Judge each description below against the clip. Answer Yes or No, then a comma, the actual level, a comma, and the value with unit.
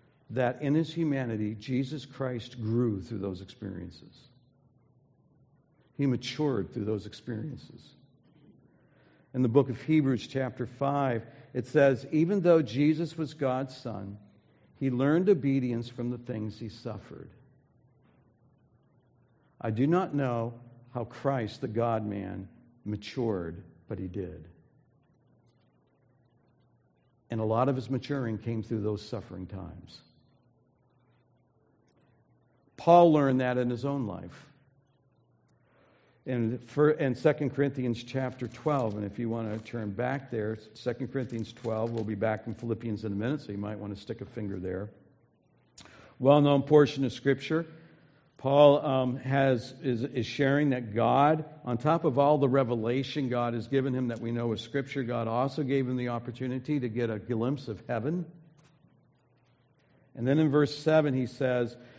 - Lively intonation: No, average, 3.6 semitones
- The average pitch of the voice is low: Yes, low, 125 Hz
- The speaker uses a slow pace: No, average, 145 wpm